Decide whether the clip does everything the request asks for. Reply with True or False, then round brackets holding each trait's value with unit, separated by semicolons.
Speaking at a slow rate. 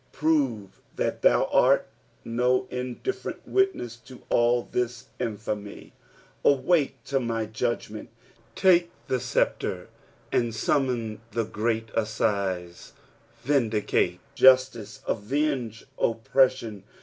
True (100 wpm)